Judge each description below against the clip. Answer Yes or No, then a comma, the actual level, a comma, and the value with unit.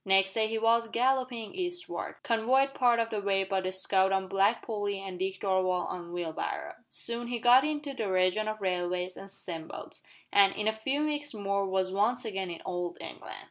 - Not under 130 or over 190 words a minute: No, average, 200 wpm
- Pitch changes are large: No, average, 3.9 semitones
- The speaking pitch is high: Yes, high, 200 Hz